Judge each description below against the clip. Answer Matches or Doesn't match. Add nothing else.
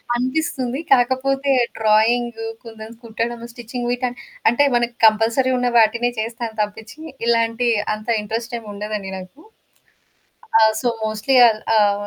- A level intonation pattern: Matches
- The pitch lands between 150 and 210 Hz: Doesn't match